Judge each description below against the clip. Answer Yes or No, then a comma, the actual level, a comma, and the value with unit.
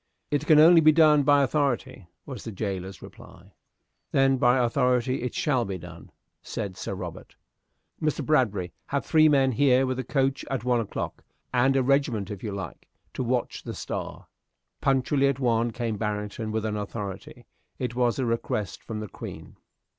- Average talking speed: Yes, average, 175 wpm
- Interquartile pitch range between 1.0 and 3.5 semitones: No, average, 4.2 semitones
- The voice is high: No, low, 125 Hz